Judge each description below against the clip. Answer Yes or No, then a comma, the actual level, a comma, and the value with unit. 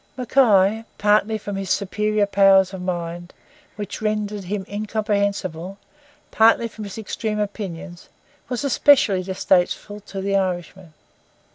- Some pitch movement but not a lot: No, narrow, 2.2 semitones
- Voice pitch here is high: Yes, high, 200 Hz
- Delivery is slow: Yes, slow, 120 wpm